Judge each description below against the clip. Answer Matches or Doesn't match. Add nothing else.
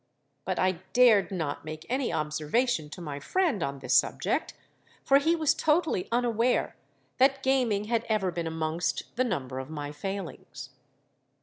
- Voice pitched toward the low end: Doesn't match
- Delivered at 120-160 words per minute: Matches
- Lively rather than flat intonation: Matches